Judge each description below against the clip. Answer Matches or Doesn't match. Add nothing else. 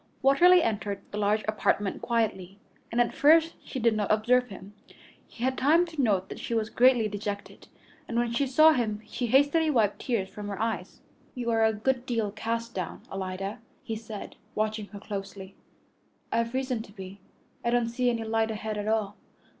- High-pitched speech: Matches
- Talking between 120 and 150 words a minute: Doesn't match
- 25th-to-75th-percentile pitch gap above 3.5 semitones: Doesn't match